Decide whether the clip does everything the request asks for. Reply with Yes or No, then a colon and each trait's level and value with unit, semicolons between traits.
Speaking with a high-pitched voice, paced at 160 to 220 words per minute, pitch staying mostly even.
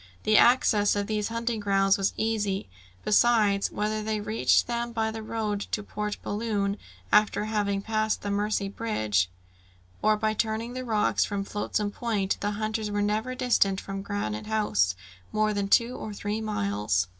Yes: high, 210 Hz; average, 165 wpm; narrow, 1.5 semitones